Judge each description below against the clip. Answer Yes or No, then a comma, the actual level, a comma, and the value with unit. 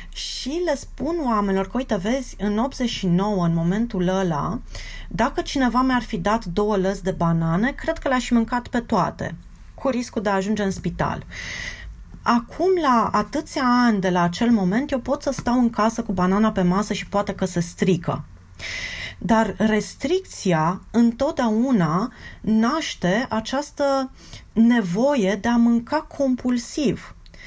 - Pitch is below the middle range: No, high, 225 Hz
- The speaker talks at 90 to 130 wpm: No, average, 145 wpm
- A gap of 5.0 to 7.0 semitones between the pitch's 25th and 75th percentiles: No, average, 4.6 semitones